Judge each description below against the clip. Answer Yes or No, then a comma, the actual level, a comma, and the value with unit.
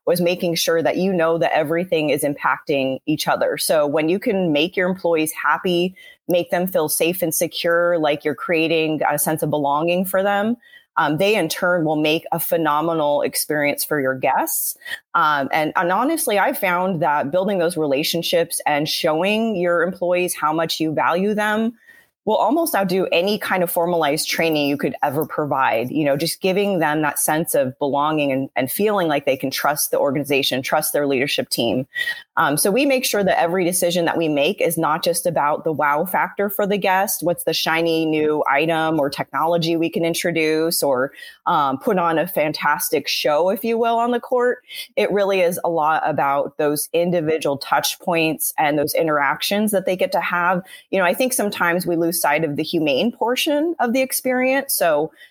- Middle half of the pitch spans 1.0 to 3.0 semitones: No, average, 4.2 semitones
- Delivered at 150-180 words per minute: No, average, 195 wpm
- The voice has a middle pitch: Yes, medium, 170 Hz